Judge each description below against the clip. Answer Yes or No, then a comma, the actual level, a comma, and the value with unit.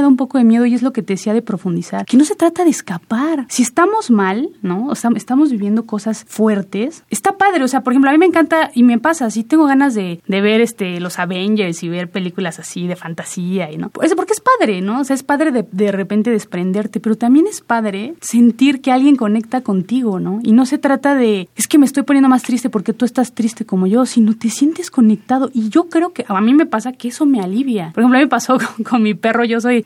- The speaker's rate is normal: No, fast, 255 wpm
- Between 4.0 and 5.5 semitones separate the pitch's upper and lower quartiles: Yes, average, 4.5 semitones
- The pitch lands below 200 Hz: No, high, 235 Hz